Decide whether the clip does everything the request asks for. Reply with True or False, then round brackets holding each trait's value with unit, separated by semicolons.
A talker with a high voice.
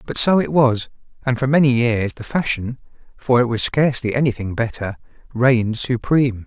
False (125 Hz)